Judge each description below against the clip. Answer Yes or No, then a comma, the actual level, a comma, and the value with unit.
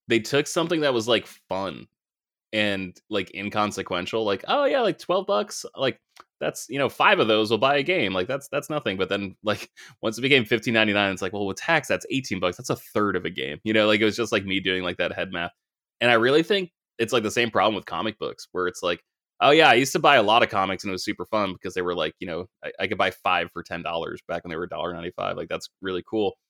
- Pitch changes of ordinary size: Yes, average, 3.3 semitones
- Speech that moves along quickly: Yes, fast, 265 wpm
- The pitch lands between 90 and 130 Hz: Yes, low, 110 Hz